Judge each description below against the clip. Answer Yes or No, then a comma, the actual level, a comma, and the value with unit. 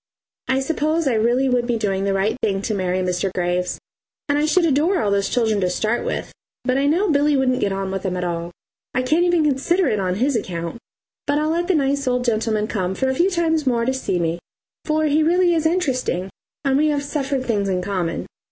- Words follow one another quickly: Yes, fast, 230 wpm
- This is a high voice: Yes, very high, 255 Hz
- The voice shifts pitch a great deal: Yes, wide, 7.5 semitones